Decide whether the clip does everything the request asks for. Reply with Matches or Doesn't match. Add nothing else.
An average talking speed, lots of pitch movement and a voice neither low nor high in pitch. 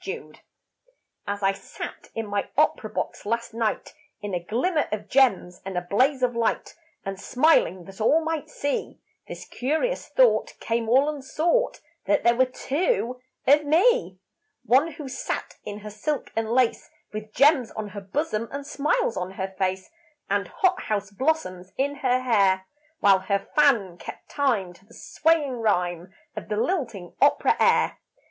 Doesn't match